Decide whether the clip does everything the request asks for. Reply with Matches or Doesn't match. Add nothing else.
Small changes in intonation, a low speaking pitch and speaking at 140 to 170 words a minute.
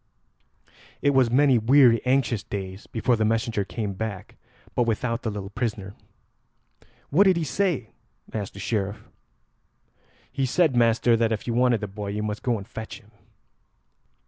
Doesn't match